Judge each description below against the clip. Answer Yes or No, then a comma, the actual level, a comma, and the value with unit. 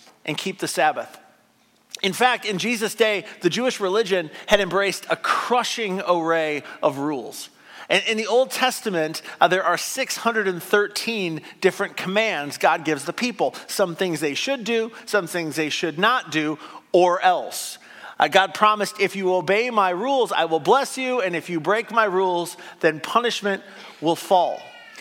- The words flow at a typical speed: Yes, average, 165 wpm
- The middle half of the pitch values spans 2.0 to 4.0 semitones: No, average, 4.8 semitones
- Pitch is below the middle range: No, high, 195 Hz